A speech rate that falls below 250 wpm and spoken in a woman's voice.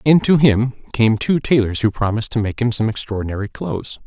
No: fast, 205 wpm; male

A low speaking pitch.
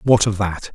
Yes: low, 100 Hz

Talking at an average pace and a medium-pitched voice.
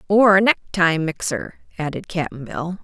Yes: average, 150 wpm; medium, 175 Hz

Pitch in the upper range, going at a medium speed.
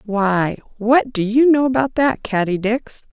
Yes: high, 230 Hz; average, 170 wpm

